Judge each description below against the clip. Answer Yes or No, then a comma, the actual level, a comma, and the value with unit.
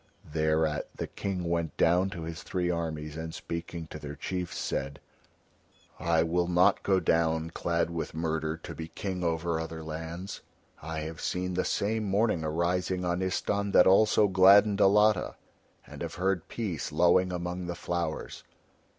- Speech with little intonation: Yes, narrow, 2.3 semitones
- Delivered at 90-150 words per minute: No, average, 160 wpm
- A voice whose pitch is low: Yes, very low, 85 Hz